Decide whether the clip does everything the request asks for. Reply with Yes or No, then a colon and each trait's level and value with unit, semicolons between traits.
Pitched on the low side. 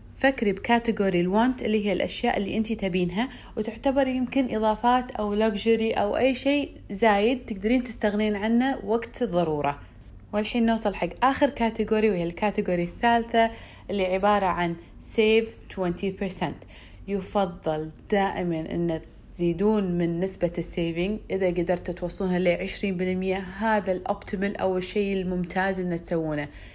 No: high, 200 Hz